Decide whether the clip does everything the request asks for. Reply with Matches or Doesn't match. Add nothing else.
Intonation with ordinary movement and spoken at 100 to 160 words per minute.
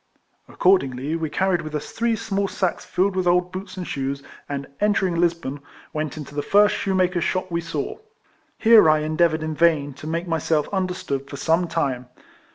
Doesn't match